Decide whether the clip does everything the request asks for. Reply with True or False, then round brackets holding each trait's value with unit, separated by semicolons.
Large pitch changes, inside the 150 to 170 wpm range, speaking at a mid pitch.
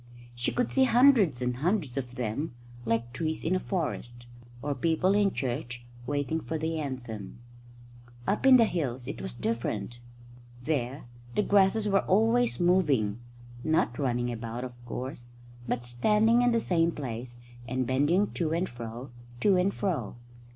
True (7.6 semitones; 155 wpm; 145 Hz)